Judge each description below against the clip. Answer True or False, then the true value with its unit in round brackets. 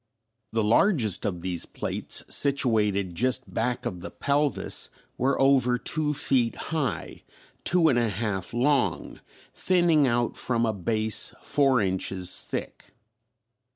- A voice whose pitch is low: True (120 Hz)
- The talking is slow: True (125 wpm)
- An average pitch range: True (4.9 semitones)